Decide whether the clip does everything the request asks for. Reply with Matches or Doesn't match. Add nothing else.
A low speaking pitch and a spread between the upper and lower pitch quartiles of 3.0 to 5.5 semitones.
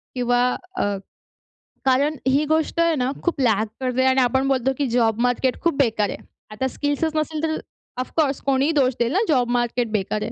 Doesn't match